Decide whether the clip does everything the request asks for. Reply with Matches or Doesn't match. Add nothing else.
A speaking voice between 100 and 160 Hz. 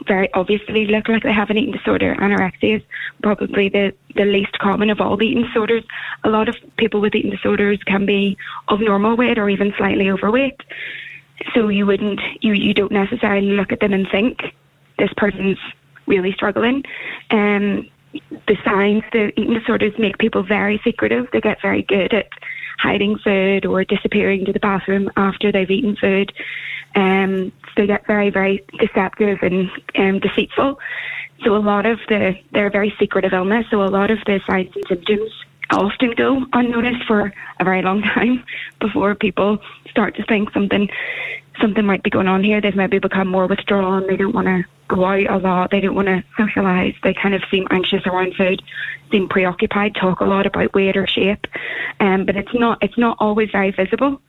Doesn't match